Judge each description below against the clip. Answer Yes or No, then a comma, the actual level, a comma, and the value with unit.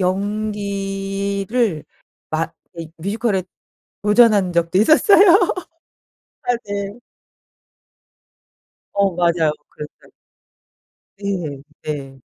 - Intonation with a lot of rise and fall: No, average, 3.6 semitones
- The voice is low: No, high, 195 Hz